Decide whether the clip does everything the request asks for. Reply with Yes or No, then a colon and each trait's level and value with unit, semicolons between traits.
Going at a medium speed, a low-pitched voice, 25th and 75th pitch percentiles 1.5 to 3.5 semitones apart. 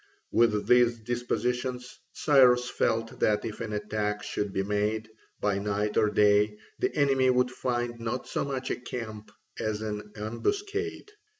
Yes: average, 145 wpm; low, 115 Hz; average, 2.9 semitones